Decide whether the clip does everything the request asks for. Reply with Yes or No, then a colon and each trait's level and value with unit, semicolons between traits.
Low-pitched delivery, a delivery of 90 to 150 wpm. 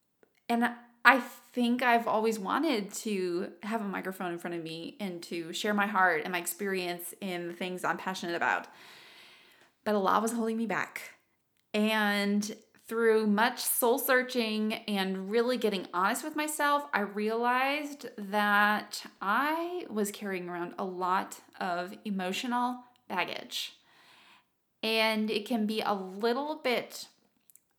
No: high, 215 Hz; average, 140 wpm